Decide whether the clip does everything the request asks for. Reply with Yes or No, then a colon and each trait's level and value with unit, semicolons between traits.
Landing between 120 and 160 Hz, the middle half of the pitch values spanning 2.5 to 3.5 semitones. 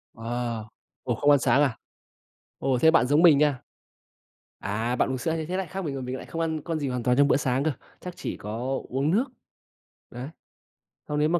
No: medium, 140 Hz; average, 4.2 semitones